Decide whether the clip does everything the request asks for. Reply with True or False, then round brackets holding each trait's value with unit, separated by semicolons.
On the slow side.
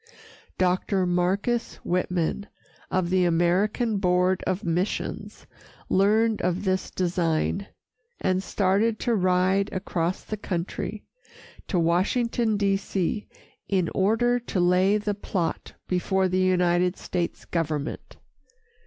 True (110 wpm)